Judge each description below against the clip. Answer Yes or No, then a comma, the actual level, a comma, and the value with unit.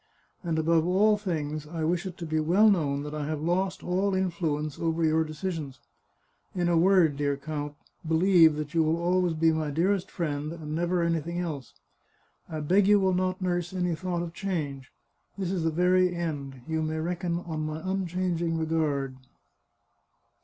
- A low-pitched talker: No, medium, 165 Hz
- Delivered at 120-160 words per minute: No, average, 180 wpm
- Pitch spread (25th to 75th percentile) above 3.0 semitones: No, average, 2.7 semitones